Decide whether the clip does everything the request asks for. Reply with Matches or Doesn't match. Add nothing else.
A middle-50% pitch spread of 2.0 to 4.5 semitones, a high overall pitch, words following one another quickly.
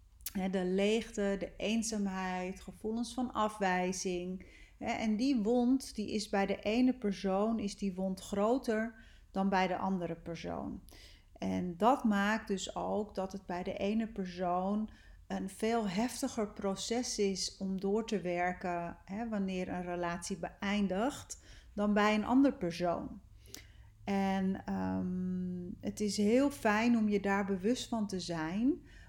Doesn't match